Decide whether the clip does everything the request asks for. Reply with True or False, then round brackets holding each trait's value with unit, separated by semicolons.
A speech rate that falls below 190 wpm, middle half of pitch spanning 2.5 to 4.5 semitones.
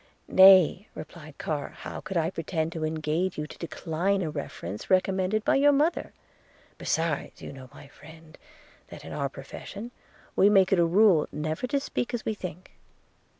True (170 wpm; 4.0 semitones)